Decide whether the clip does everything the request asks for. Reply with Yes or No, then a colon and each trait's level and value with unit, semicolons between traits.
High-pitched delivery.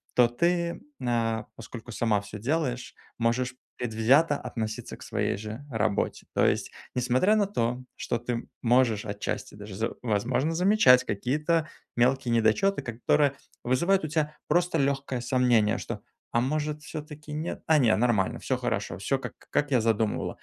No: low, 125 Hz